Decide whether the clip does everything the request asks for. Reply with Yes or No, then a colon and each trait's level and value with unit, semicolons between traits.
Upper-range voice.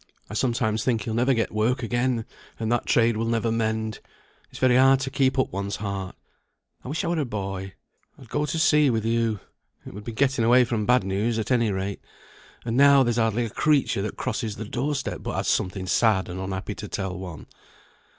No: low, 115 Hz